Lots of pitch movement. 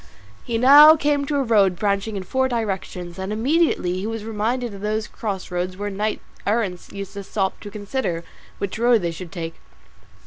No: average, 3.8 semitones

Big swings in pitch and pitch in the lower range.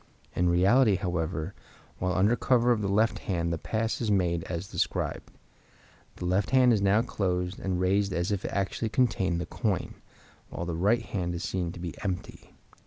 No: average, 3.3 semitones; very low, 95 Hz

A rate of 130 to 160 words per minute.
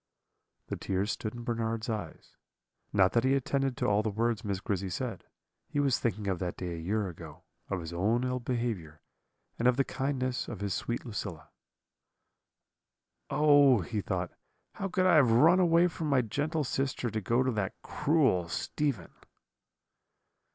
No: average, 170 wpm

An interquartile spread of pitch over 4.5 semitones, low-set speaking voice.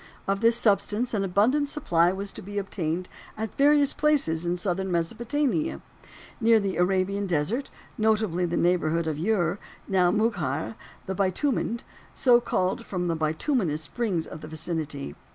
No: average, 4.9 semitones; high, 190 Hz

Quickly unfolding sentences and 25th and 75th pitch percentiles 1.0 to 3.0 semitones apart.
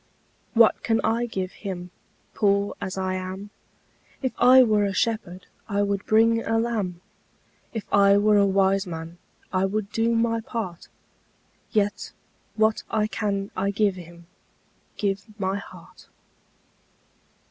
No: slow, 135 wpm; average, 2.7 semitones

